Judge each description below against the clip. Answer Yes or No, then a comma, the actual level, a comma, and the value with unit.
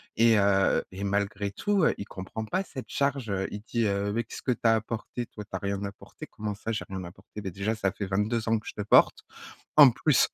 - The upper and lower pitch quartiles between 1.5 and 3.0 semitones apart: Yes, narrow, 2.6 semitones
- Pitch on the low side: Yes, low, 105 Hz